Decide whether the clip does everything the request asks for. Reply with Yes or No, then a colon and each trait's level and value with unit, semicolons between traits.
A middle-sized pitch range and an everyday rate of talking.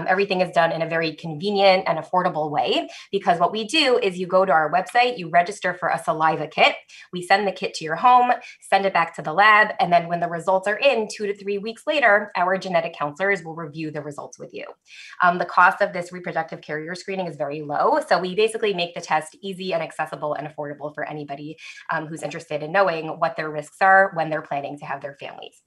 No: average, 3.8 semitones; fast, 235 wpm